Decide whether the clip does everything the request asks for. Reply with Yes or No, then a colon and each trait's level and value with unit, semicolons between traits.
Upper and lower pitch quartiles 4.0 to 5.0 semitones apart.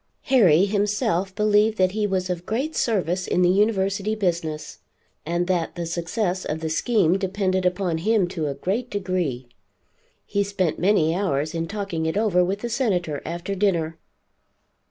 No: average, 3.4 semitones